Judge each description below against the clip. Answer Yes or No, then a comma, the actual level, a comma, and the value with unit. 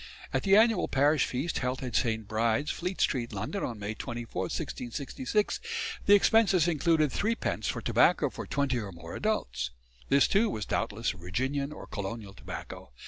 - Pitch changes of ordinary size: No, wide, 7.8 semitones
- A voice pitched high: No, low, 130 Hz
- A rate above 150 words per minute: Yes, average, 160 wpm